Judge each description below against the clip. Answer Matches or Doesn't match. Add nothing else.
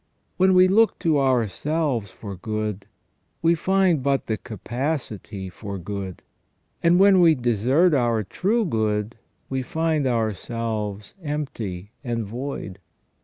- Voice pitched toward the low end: Matches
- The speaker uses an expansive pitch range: Matches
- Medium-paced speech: Doesn't match